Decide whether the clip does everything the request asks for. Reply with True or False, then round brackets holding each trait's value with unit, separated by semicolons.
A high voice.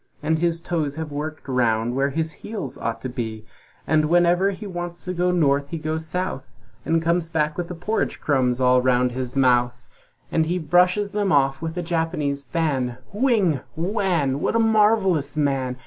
False (160 Hz)